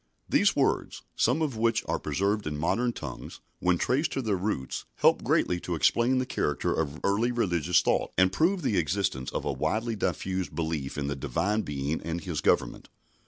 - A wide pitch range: Yes, wide, 6.6 semitones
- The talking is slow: No, average, 185 wpm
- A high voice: No, very low, 95 Hz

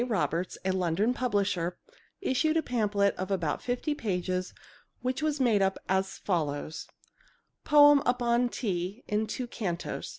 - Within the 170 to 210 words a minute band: No, slow, 135 wpm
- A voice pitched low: No, high, 205 Hz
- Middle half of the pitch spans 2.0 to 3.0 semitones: No, average, 5.3 semitones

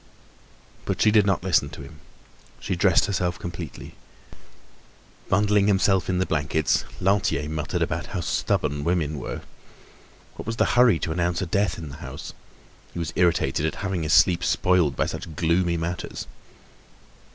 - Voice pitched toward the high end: No, very low, 85 Hz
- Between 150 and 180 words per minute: Yes, average, 160 wpm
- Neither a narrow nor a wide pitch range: Yes, average, 3.3 semitones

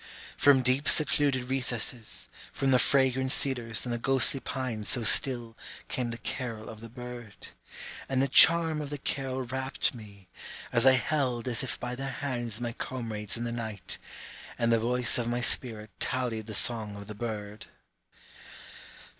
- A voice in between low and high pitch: No, low, 120 Hz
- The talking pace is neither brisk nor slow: Yes, average, 165 wpm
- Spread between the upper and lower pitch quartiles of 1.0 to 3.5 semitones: Yes, narrow, 2.6 semitones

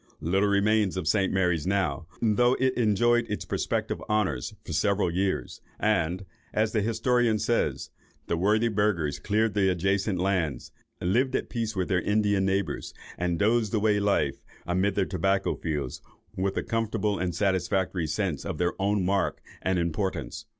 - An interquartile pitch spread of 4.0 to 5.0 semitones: No, average, 3.0 semitones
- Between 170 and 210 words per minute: No, average, 155 wpm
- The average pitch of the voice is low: Yes, low, 100 Hz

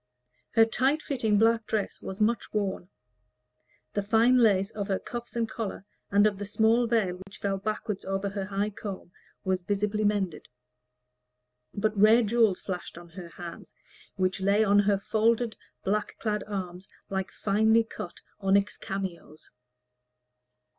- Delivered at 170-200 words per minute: No, average, 145 wpm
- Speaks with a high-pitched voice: Yes, high, 205 Hz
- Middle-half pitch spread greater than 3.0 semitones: No, narrow, 2.4 semitones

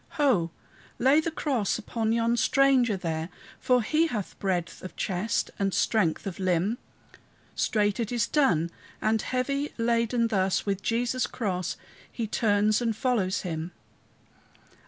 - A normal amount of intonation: Yes, average, 4.5 semitones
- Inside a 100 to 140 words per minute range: Yes, slow, 135 wpm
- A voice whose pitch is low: No, high, 220 Hz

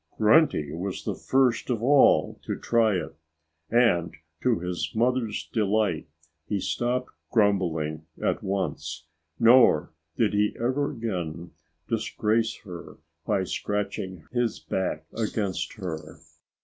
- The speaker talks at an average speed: No, slow, 115 wpm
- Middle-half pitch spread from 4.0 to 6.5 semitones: Yes, average, 5.0 semitones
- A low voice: Yes, low, 105 Hz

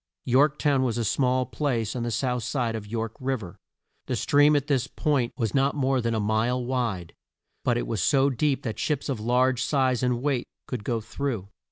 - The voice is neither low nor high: No, low, 125 Hz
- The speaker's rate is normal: No, fast, 210 wpm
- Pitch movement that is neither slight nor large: Yes, average, 3.0 semitones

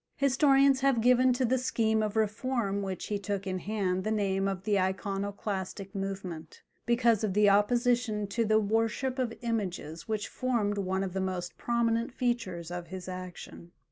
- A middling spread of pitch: Yes, average, 3.7 semitones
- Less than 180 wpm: Yes, average, 170 wpm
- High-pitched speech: Yes, high, 210 Hz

